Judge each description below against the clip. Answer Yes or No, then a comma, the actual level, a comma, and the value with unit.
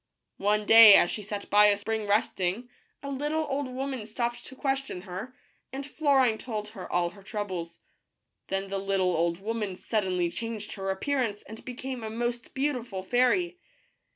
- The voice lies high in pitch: Yes, high, 220 Hz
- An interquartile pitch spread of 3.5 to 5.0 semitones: Yes, average, 4.7 semitones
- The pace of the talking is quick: No, average, 165 wpm